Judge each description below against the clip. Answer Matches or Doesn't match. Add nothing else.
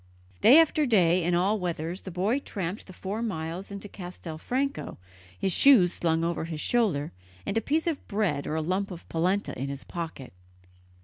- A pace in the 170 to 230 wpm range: Matches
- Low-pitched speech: Doesn't match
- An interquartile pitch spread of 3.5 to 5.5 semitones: Matches